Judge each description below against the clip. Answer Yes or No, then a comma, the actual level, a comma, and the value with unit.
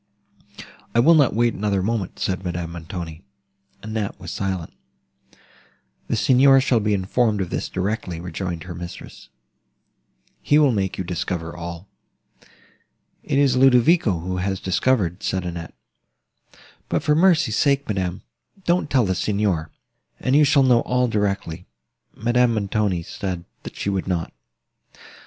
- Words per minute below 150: Yes, average, 140 wpm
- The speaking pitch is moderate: No, low, 100 Hz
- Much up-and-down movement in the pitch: Yes, wide, 5.7 semitones